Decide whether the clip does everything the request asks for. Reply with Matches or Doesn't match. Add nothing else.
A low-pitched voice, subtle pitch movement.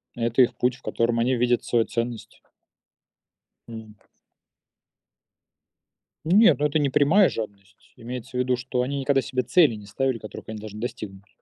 Doesn't match